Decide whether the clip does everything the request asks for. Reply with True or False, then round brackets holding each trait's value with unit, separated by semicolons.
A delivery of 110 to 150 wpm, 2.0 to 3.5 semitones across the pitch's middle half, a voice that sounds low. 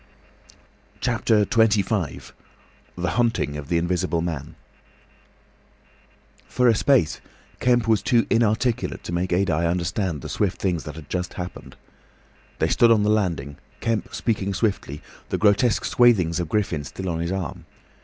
False (145 wpm; 4.8 semitones; 95 Hz)